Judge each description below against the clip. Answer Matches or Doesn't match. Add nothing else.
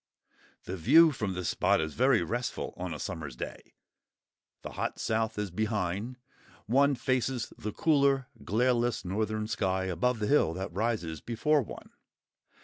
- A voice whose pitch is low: Matches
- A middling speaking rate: Matches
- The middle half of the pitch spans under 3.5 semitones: Doesn't match